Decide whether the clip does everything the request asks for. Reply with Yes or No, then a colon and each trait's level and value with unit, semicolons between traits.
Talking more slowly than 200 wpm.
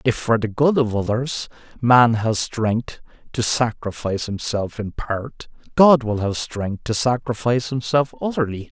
Yes: average, 150 wpm